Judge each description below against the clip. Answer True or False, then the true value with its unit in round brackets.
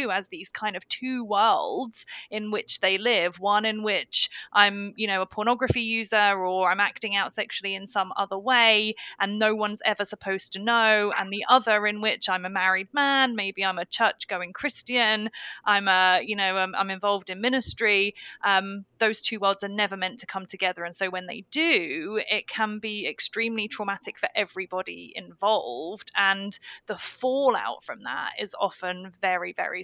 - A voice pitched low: False (205 Hz)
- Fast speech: False (180 wpm)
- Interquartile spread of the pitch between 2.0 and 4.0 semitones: True (2.4 semitones)